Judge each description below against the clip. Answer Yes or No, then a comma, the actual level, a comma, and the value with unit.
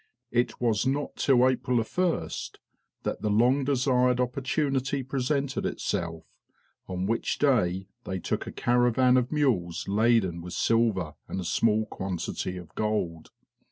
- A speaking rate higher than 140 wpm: No, slow, 135 wpm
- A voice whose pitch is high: No, low, 120 Hz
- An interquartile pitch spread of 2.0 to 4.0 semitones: No, wide, 5.5 semitones